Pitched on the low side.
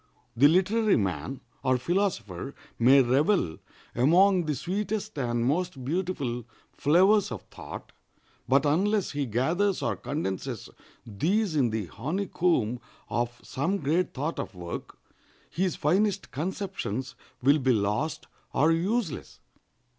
No: medium, 150 Hz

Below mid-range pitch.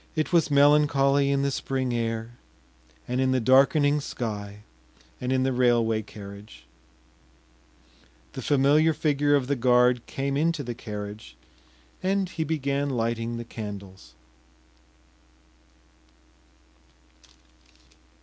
Yes: low, 130 Hz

